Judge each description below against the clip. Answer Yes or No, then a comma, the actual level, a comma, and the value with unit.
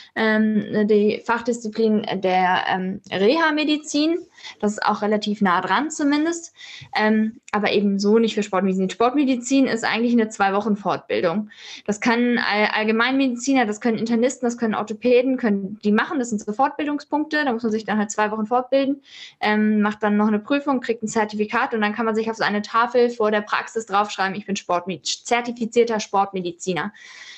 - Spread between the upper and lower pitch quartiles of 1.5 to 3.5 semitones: Yes, average, 3.2 semitones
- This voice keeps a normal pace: Yes, average, 165 wpm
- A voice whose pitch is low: No, high, 220 Hz